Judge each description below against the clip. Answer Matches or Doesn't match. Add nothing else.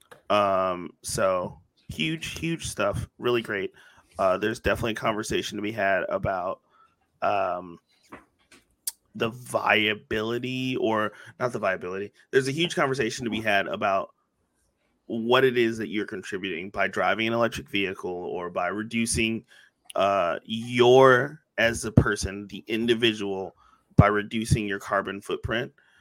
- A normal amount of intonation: Matches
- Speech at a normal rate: Doesn't match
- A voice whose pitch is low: Matches